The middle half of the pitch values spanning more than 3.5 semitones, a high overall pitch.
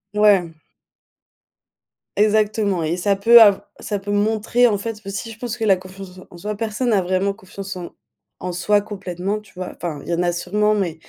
No: narrow, 2.5 semitones; high, 200 Hz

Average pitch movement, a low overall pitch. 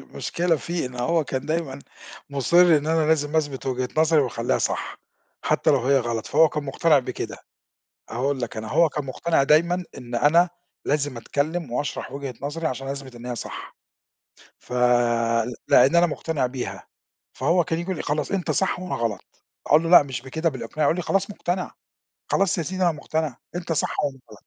No: average, 4.1 semitones; medium, 150 Hz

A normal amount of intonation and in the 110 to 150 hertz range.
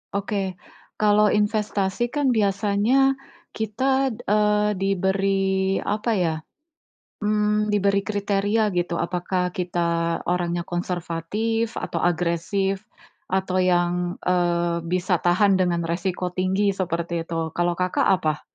No: average, 3.0 semitones; high, 190 Hz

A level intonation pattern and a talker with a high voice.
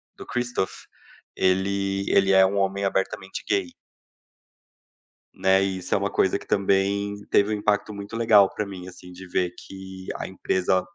No: narrow, 1.1 semitones; very low, 95 Hz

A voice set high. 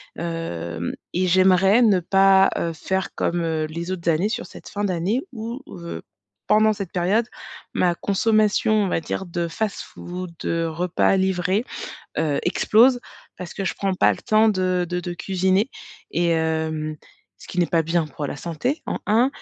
No: medium, 180 Hz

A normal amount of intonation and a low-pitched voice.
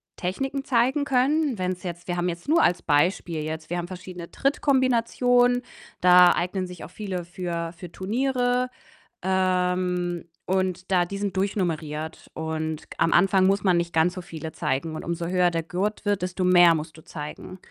No: average, 3.0 semitones; medium, 180 Hz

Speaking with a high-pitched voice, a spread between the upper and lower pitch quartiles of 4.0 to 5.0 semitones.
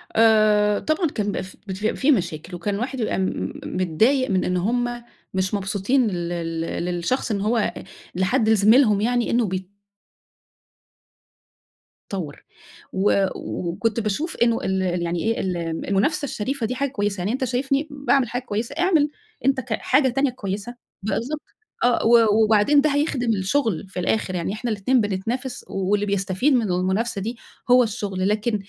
Yes: high, 215 Hz; average, 4.6 semitones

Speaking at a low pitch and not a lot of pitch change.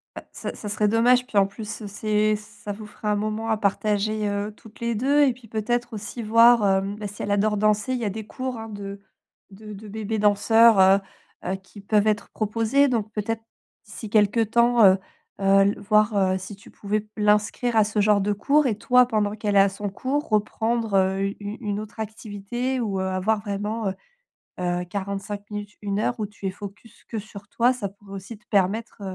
No: high, 210 Hz; narrow, 1.8 semitones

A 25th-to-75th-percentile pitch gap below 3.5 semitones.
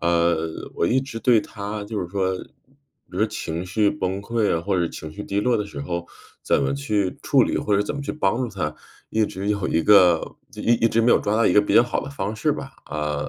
No: average, 4.2 semitones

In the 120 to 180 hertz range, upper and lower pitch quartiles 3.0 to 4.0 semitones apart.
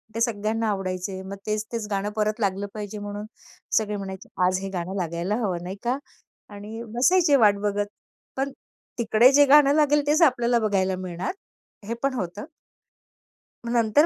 No: high, 210 Hz; average, 3.7 semitones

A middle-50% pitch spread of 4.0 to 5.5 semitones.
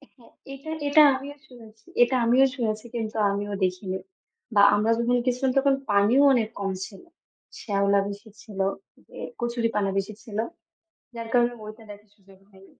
No: average, 3.2 semitones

